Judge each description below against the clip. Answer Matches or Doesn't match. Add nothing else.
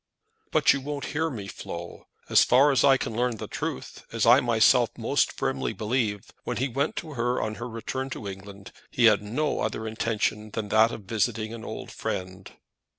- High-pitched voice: Doesn't match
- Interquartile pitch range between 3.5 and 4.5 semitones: Matches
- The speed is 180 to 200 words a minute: Matches